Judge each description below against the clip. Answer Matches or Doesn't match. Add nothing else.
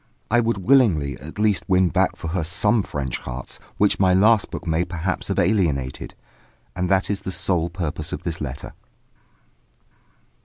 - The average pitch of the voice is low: Matches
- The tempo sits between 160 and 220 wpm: Matches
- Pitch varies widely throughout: Doesn't match